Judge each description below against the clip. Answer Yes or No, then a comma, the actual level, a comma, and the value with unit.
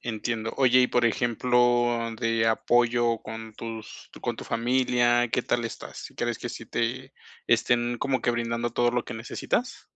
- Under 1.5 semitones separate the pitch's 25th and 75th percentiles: Yes, narrow, 1.0 semitones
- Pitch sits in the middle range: No, low, 120 Hz